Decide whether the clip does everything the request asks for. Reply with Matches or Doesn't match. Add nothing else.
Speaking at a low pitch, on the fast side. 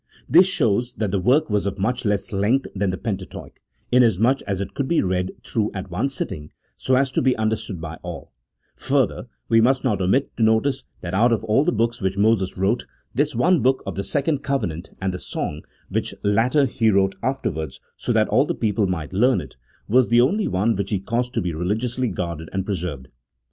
Matches